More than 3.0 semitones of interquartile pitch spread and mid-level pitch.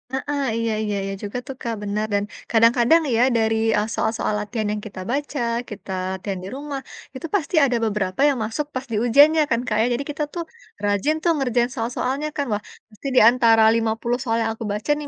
No: average, 4.4 semitones; high, 230 Hz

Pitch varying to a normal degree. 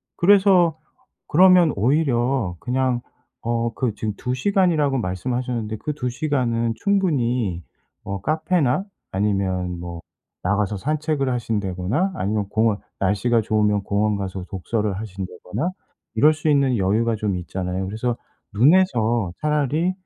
No: wide, 6.5 semitones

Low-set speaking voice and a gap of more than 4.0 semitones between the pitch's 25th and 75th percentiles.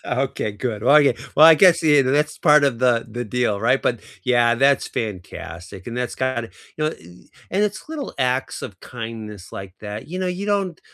Yes: low, 125 Hz; average, 5.1 semitones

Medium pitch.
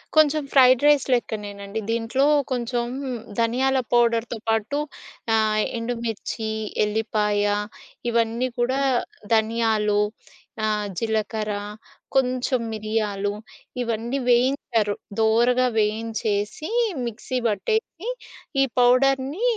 No: high, 230 Hz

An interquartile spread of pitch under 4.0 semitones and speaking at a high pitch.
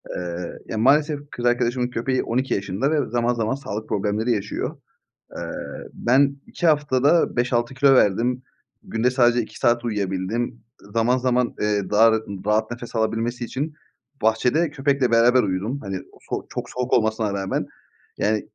No: average, 2.8 semitones; low, 120 Hz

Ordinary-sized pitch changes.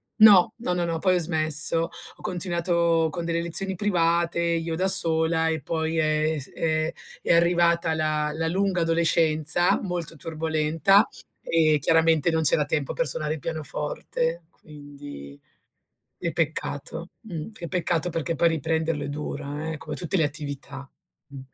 No: narrow, 1.8 semitones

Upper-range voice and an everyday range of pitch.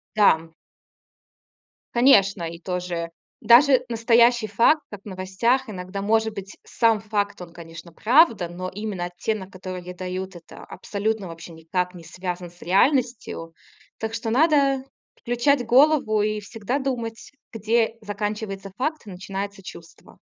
Yes: high, 205 Hz; average, 4.3 semitones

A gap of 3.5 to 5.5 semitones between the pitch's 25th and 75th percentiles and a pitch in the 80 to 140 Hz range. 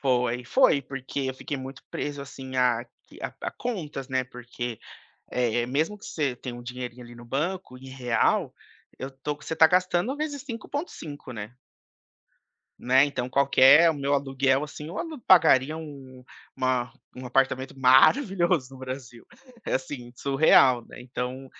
No: average, 3.1 semitones; low, 135 Hz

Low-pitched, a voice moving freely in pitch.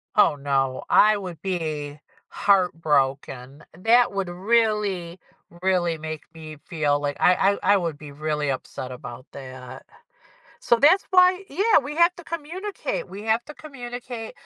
No: medium, 180 Hz; wide, 8.2 semitones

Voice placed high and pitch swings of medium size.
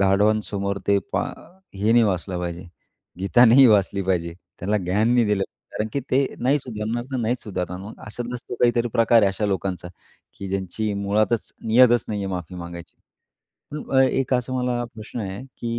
No: low, 105 Hz; average, 3.8 semitones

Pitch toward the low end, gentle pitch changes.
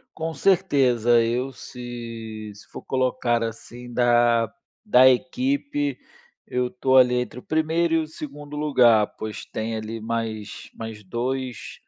No: low, 125 Hz; average, 3.9 semitones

